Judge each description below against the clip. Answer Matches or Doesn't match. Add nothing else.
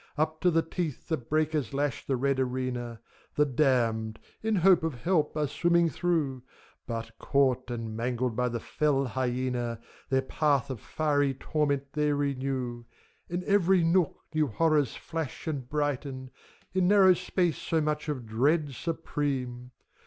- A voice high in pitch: Doesn't match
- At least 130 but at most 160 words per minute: Matches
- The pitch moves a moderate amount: Matches